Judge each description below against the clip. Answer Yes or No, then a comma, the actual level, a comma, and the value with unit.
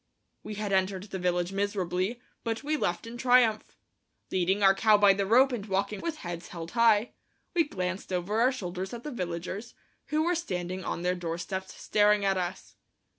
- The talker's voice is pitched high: Yes, high, 195 Hz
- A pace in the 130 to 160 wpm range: No, average, 180 wpm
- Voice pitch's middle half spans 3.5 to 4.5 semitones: Yes, average, 4.0 semitones